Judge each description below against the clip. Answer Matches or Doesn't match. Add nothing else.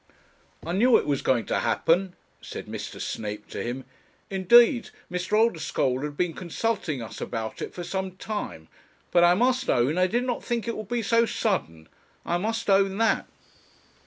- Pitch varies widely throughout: Matches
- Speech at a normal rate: Matches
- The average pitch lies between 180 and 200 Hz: Matches